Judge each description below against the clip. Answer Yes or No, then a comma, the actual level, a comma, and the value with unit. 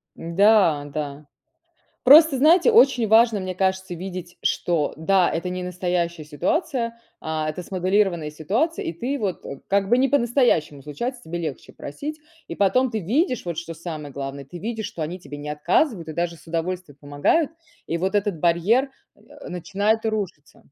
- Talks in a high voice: No, medium, 180 Hz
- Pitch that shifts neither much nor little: No, wide, 5.9 semitones